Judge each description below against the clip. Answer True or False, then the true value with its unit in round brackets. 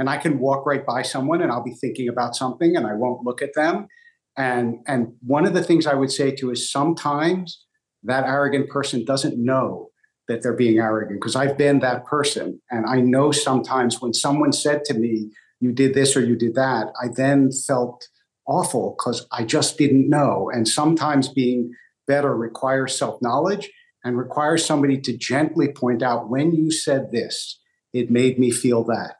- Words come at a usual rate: True (190 wpm)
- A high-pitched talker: False (135 Hz)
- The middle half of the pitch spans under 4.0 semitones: True (2.9 semitones)